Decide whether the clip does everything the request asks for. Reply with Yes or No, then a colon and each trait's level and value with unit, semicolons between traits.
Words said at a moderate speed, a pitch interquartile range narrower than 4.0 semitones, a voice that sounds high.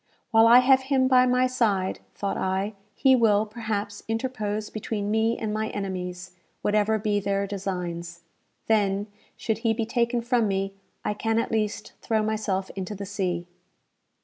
Yes: average, 160 wpm; narrow, 2.6 semitones; high, 215 Hz